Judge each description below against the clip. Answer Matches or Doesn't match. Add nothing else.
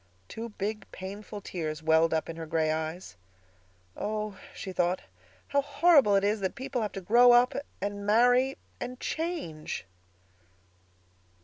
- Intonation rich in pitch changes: Matches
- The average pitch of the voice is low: Doesn't match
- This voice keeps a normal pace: Doesn't match